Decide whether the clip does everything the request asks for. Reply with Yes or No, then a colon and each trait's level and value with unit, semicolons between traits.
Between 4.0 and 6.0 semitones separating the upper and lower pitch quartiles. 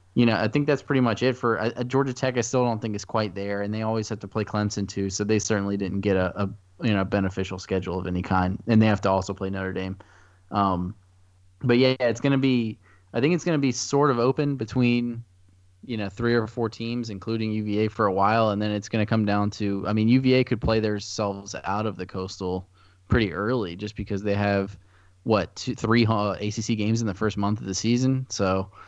No: average, 3.2 semitones